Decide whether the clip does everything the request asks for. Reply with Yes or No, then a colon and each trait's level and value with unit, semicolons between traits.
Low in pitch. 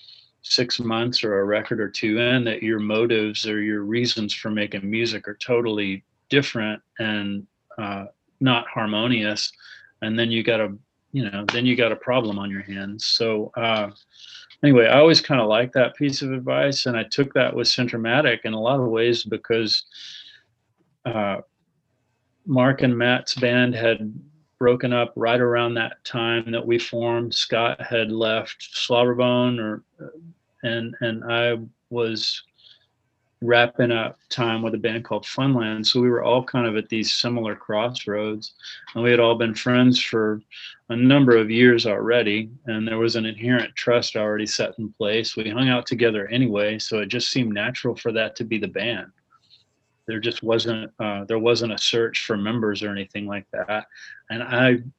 Yes: low, 115 Hz